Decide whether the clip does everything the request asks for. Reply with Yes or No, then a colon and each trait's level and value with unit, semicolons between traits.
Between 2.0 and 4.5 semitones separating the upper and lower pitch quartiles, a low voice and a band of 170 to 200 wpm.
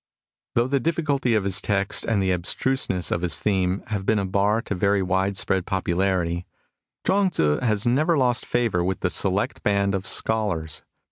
Yes: average, 3.8 semitones; low, 100 Hz; average, 180 wpm